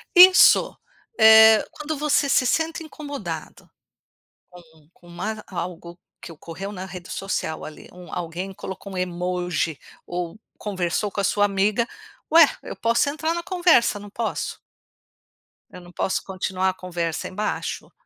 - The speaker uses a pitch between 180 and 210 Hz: Yes, high, 195 Hz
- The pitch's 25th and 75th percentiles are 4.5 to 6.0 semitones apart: Yes, average, 4.8 semitones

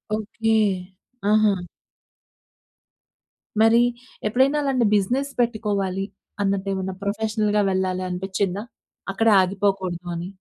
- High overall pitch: Yes, high, 200 Hz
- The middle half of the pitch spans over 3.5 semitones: No, average, 2.7 semitones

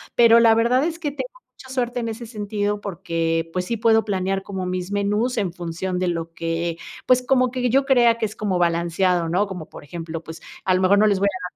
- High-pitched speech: Yes, high, 200 Hz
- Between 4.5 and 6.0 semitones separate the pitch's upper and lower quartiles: Yes, average, 4.8 semitones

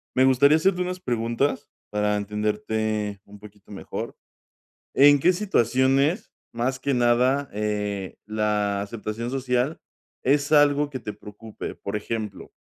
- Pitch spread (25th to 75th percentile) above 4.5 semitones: Yes, average, 4.9 semitones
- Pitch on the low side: Yes, low, 115 Hz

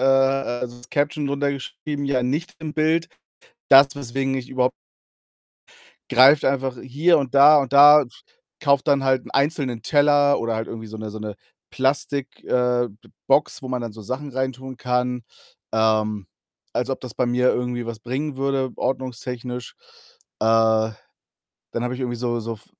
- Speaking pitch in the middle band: No, low, 130 Hz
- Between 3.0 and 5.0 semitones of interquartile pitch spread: No, narrow, 2.6 semitones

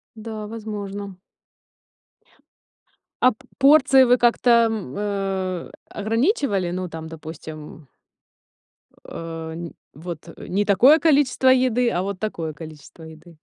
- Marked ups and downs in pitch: Yes, wide, 6.2 semitones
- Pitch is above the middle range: Yes, high, 200 Hz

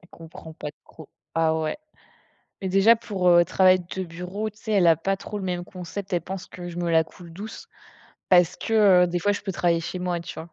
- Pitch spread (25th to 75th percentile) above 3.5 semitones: No, narrow, 2.4 semitones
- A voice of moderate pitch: Yes, medium, 180 Hz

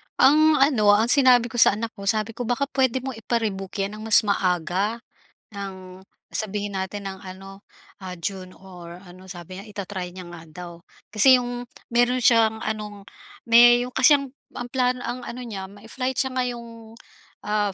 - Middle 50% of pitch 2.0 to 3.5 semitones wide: No, average, 4.1 semitones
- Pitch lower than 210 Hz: No, high, 215 Hz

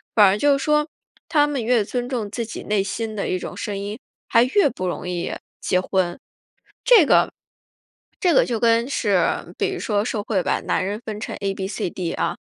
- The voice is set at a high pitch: Yes, high, 220 Hz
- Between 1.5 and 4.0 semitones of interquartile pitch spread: No, average, 4.4 semitones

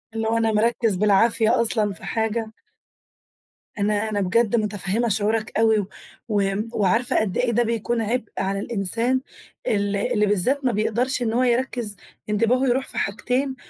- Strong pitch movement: No, narrow, 2.6 semitones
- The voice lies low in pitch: No, high, 220 Hz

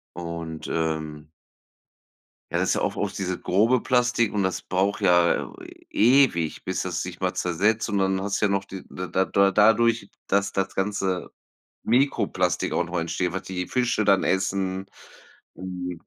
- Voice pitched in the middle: No, very low, 95 Hz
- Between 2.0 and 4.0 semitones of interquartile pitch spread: Yes, narrow, 2.4 semitones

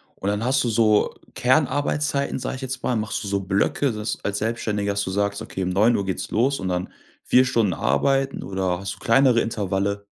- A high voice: No, low, 105 Hz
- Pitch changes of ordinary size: Yes, average, 4.5 semitones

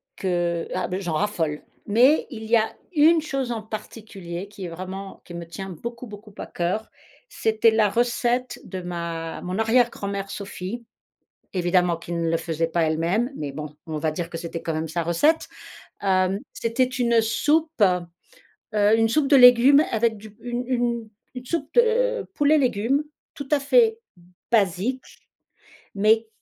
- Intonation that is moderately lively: No, wide, 5.8 semitones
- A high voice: Yes, high, 215 Hz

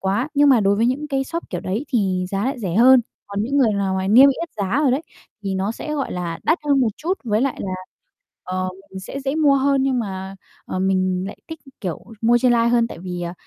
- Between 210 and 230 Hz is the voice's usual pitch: Yes, high, 225 Hz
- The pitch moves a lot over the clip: Yes, wide, 6.1 semitones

